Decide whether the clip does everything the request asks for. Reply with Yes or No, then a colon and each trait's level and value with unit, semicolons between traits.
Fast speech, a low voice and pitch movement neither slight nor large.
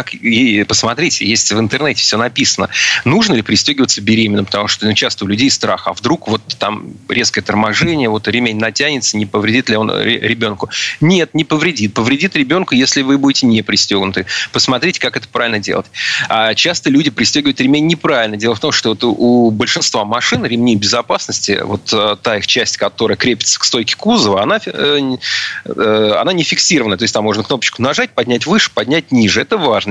No: fast, 175 wpm; low, 120 Hz; wide, 5.8 semitones